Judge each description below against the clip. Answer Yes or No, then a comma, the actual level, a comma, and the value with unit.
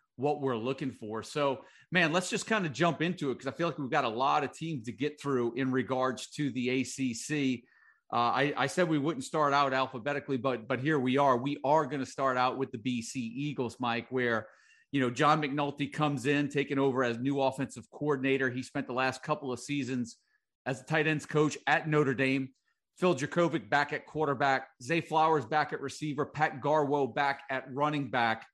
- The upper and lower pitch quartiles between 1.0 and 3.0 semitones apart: Yes, narrow, 2.4 semitones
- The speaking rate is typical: No, fast, 210 wpm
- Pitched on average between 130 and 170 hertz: Yes, medium, 140 Hz